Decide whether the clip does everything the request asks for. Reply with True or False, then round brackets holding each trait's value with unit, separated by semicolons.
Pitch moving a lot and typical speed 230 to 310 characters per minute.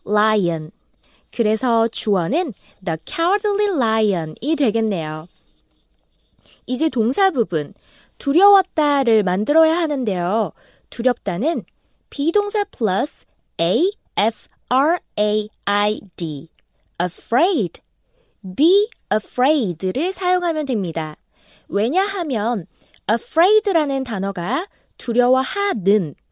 True (8.9 semitones; 245 characters per minute)